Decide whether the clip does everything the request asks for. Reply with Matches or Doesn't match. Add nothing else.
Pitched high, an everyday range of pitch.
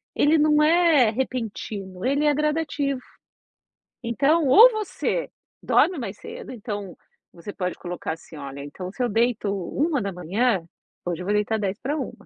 Doesn't match